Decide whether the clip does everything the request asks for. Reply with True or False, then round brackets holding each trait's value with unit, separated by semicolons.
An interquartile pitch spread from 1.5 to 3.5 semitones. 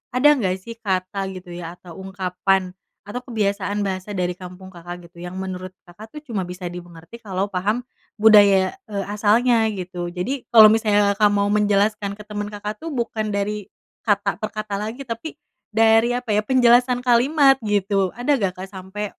True (3.0 semitones)